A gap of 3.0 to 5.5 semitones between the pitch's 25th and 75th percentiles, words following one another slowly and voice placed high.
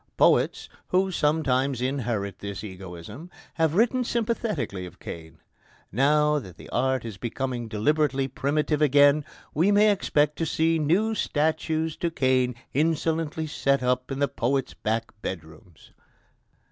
No: average, 5.2 semitones; slow, 130 wpm; medium, 140 Hz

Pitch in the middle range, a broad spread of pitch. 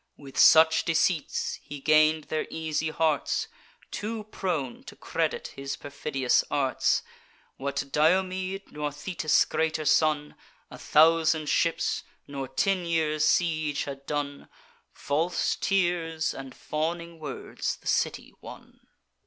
No: medium, 155 Hz; narrow, 2.5 semitones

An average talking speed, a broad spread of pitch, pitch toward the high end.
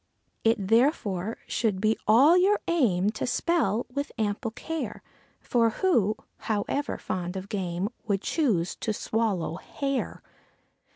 No: slow, 125 wpm; wide, 5.8 semitones; high, 225 Hz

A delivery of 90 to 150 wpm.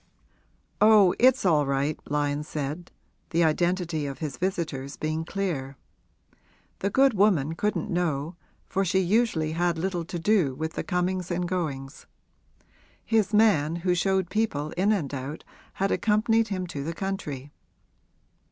Yes: average, 145 wpm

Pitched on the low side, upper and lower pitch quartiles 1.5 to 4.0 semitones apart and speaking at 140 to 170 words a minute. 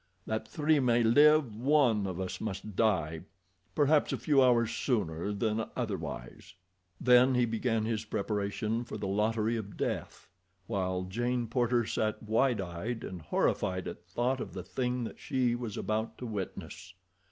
Yes: low, 115 Hz; average, 3.5 semitones; average, 155 wpm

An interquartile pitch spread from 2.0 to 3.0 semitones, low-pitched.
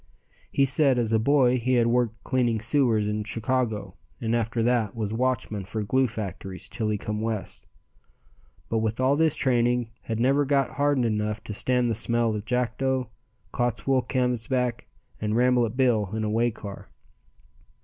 Yes: average, 2.7 semitones; low, 120 Hz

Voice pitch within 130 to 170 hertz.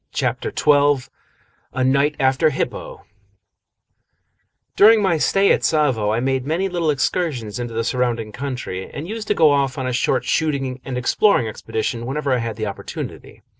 Yes: low, 135 Hz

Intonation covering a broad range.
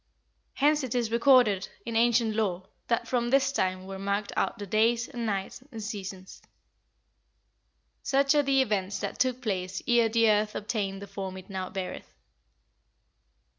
No: average, 3.7 semitones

